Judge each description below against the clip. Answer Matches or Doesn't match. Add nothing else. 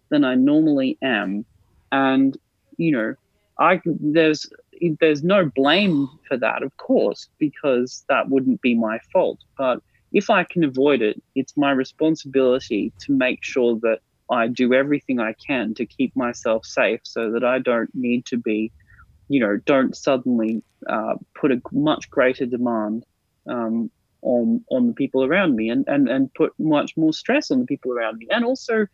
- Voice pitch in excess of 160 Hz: Doesn't match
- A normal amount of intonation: Doesn't match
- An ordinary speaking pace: Matches